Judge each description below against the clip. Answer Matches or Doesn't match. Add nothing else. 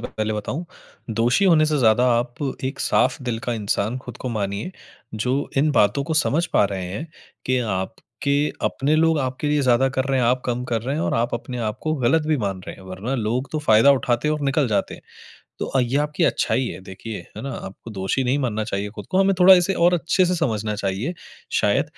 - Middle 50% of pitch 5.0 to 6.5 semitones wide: Matches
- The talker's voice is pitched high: Doesn't match